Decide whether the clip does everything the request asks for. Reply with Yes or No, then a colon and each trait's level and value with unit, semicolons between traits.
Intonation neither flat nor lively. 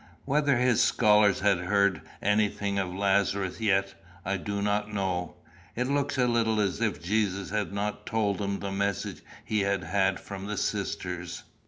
No: narrow, 1.5 semitones